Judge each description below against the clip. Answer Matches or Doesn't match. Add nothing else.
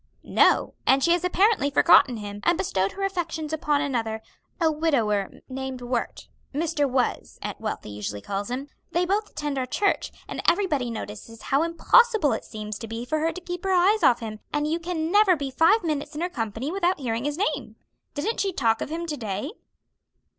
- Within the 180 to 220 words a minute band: Matches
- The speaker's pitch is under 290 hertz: Doesn't match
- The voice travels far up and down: Matches